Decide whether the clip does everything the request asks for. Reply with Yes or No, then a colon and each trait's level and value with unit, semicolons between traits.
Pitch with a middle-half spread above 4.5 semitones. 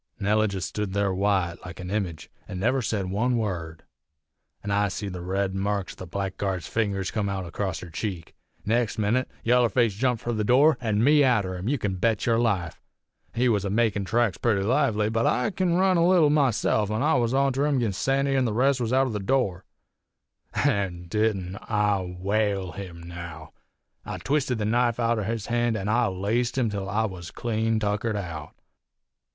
No: average, 3.9 semitones